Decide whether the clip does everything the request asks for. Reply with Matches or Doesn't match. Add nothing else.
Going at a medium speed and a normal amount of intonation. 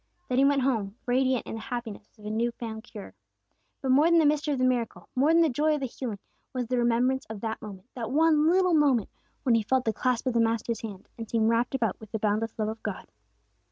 Doesn't match